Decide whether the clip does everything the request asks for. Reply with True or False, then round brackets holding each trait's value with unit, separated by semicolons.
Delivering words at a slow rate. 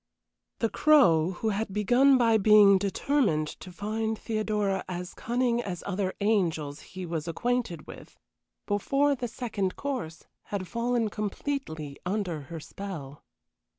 True (130 wpm)